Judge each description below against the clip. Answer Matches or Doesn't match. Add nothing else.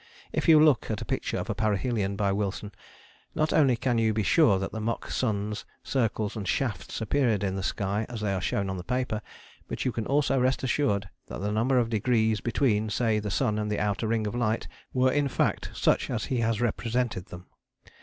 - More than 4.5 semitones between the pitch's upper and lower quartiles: Doesn't match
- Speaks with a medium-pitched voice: Doesn't match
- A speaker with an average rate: Doesn't match